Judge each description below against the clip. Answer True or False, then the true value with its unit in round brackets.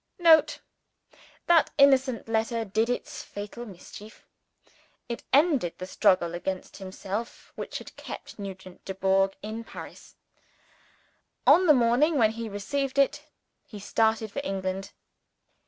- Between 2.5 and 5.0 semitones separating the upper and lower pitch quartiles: False (5.6 semitones)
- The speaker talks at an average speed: False (120 wpm)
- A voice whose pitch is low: False (220 Hz)